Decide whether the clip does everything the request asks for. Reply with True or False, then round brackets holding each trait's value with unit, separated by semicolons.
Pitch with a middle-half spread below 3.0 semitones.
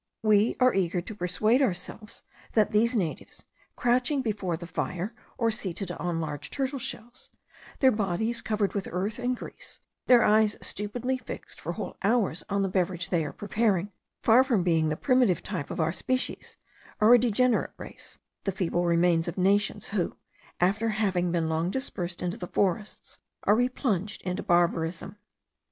False (4.6 semitones)